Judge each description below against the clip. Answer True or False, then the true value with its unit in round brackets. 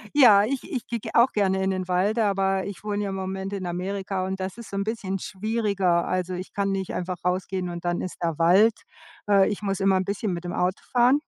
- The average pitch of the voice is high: True (195 Hz)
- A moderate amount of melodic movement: False (2.0 semitones)